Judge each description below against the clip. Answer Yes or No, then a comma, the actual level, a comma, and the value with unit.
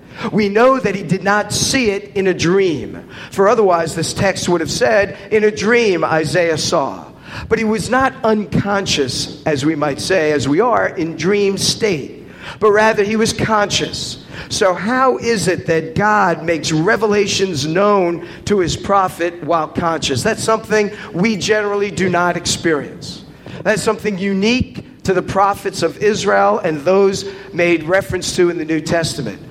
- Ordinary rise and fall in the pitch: Yes, average, 4.0 semitones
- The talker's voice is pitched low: No, high, 195 Hz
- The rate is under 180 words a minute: Yes, average, 165 wpm